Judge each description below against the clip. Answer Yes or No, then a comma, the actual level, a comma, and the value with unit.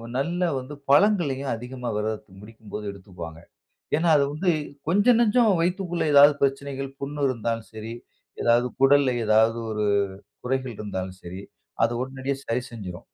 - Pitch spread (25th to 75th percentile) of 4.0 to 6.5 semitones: Yes, average, 4.7 semitones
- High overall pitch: No, low, 130 Hz